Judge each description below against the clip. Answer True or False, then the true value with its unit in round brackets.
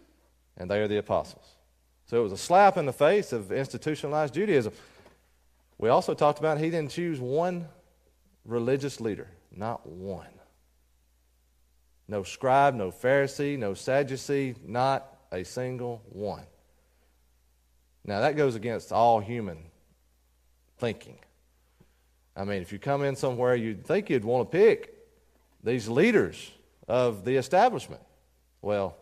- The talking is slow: True (130 wpm)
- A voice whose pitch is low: True (105 Hz)